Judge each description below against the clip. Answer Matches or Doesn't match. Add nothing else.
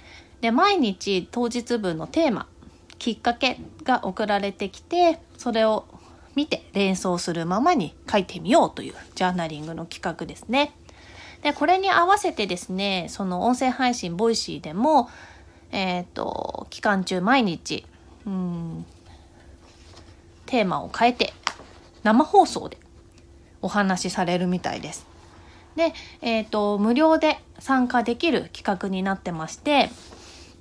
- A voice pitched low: Doesn't match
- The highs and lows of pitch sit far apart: Matches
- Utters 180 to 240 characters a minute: Doesn't match